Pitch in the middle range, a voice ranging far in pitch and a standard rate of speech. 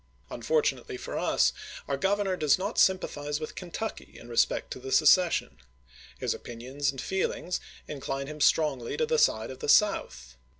Yes: medium, 155 Hz; wide, 6.0 semitones; average, 160 wpm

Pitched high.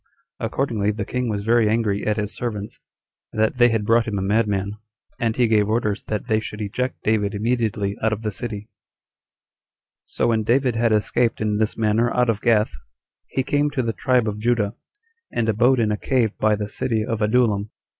No: low, 110 Hz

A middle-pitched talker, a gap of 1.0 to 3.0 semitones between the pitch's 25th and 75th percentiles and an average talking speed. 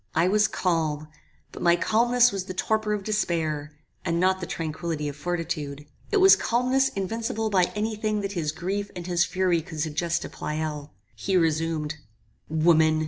No: medium, 175 Hz; average, 4.8 semitones; average, 170 wpm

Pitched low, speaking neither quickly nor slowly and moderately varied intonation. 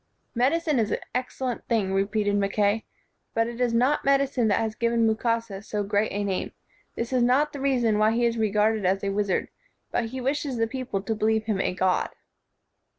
No: high, 225 Hz; average, 195 wpm; average, 3.3 semitones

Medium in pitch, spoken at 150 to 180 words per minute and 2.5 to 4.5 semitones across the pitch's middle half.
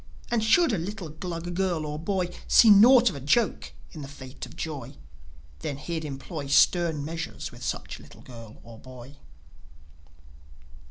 No: medium, 160 Hz; average, 160 wpm; average, 5.3 semitones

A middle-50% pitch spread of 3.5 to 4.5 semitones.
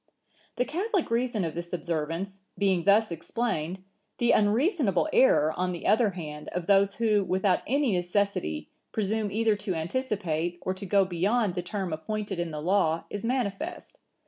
Yes: average, 4.0 semitones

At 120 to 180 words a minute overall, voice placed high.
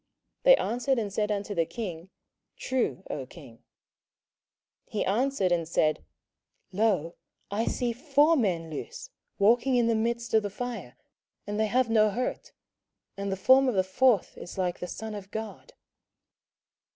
Yes: average, 160 wpm; high, 220 Hz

